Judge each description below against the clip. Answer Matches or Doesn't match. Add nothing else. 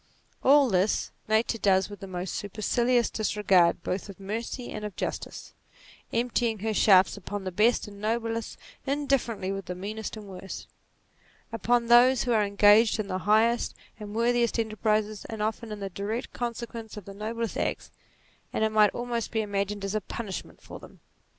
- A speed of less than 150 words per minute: Doesn't match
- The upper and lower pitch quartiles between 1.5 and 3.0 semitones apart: Matches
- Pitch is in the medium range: Doesn't match